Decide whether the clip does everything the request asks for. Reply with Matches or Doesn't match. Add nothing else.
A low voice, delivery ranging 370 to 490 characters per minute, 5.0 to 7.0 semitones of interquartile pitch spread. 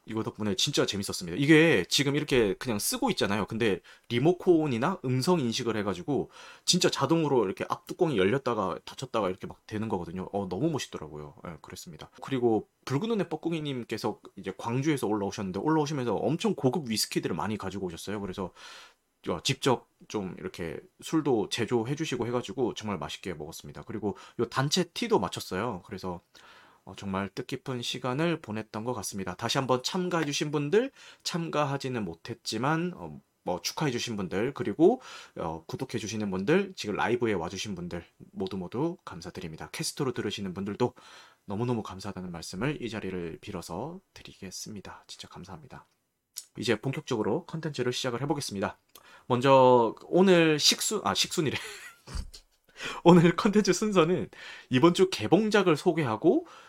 Doesn't match